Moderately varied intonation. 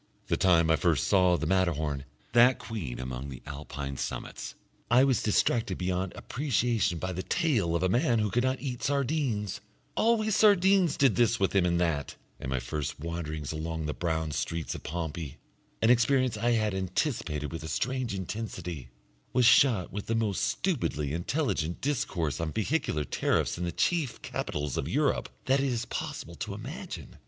No: wide, 7.5 semitones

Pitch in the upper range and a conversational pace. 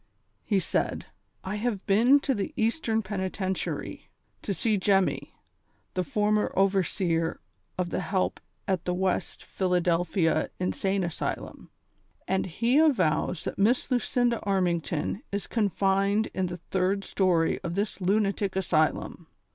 No: high, 195 Hz; slow, 130 wpm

